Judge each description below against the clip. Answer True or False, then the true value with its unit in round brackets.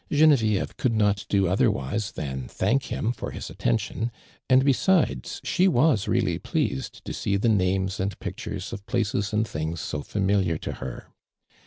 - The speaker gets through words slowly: False (160 wpm)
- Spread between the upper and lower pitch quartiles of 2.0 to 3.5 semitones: False (4.2 semitones)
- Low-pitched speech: True (100 Hz)